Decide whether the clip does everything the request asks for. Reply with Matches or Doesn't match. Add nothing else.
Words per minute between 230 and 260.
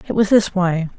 Matches